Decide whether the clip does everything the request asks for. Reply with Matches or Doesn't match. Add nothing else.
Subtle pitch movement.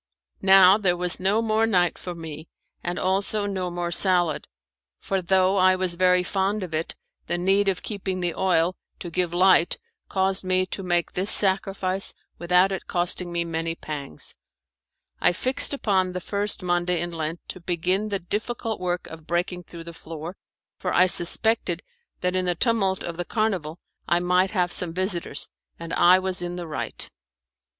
Matches